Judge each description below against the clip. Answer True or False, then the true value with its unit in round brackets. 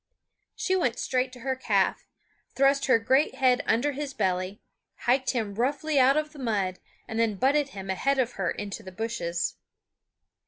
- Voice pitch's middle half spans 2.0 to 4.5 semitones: False (5.0 semitones)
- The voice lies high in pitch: True (250 Hz)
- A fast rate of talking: False (170 wpm)